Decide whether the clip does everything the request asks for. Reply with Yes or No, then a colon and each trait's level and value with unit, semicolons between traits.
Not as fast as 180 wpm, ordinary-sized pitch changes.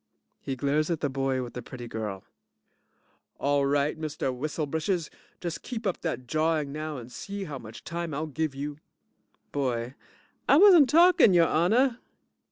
Yes: average, 165 wpm; average, 4.2 semitones